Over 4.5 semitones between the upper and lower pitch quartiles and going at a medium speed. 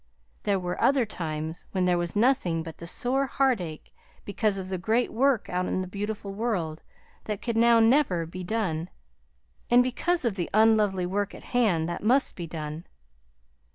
Yes: average, 5.1 semitones; average, 175 wpm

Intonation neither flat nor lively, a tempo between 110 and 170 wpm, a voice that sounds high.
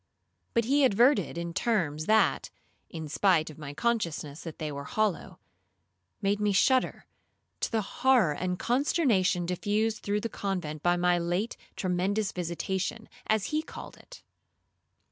Yes: average, 4.6 semitones; average, 145 wpm; high, 195 Hz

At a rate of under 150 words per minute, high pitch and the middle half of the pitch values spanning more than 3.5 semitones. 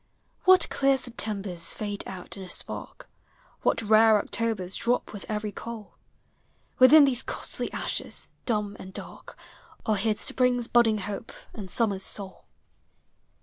No: average, 140 wpm; high, 215 Hz; average, 3.0 semitones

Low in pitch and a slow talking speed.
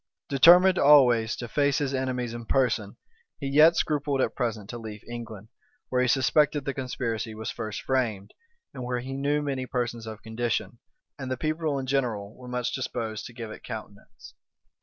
No: low, 125 Hz; average, 180 wpm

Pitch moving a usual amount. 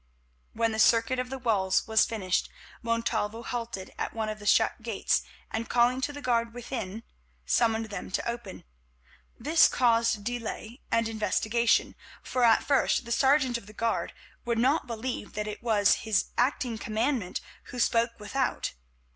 No: narrow, 1.9 semitones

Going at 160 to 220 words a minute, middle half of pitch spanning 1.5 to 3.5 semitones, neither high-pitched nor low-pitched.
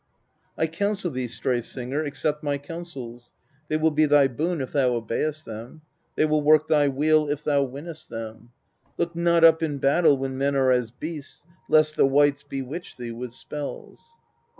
Yes: average, 180 wpm; average, 3.2 semitones; medium, 145 Hz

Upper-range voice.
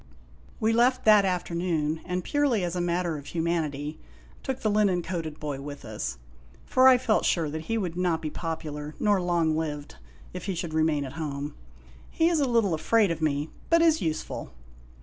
No: medium, 170 Hz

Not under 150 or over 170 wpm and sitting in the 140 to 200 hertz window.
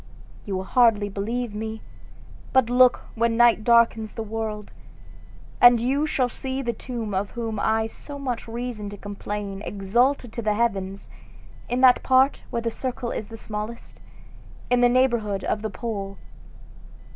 No: average, 160 wpm; high, 225 Hz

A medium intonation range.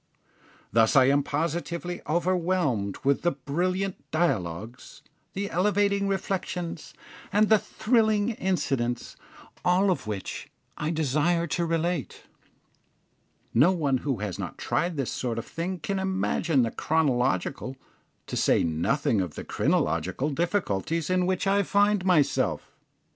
No: wide, 5.9 semitones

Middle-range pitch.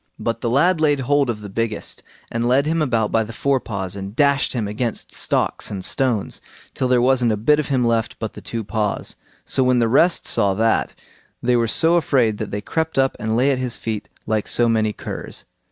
No: low, 120 Hz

